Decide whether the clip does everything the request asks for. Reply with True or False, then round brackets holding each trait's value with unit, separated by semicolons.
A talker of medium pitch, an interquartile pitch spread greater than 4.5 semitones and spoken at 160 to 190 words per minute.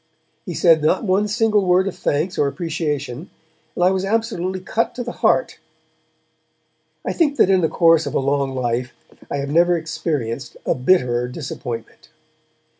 True (165 Hz; 5.3 semitones; 165 wpm)